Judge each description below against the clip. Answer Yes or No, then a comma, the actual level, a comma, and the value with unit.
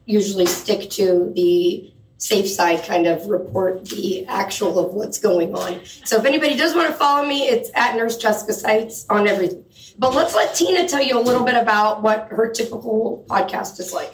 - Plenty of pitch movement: Yes, wide, 6.1 semitones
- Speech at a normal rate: Yes, average, 195 wpm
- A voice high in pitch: Yes, high, 220 Hz